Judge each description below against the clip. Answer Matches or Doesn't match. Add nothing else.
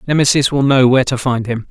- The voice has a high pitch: Doesn't match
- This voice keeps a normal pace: Doesn't match